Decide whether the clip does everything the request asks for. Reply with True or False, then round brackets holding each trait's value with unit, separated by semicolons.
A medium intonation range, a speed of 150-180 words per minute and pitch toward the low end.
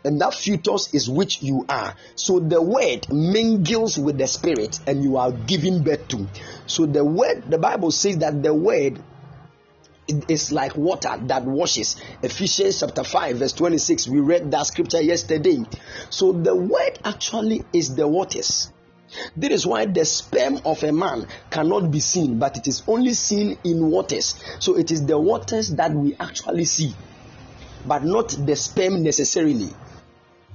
False (3.9 semitones; 165 wpm; 155 Hz)